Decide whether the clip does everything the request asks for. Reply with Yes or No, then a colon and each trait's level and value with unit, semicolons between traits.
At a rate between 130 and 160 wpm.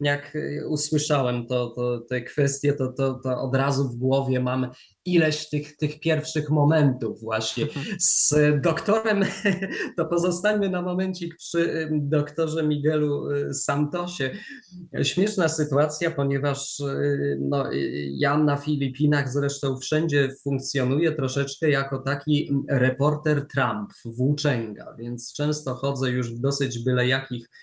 No: average, 115 wpm